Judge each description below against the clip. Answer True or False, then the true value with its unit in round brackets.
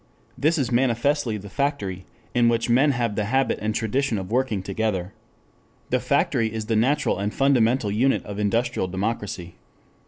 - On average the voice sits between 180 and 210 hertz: False (115 Hz)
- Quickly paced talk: False (160 wpm)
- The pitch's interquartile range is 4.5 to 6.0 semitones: False (4.1 semitones)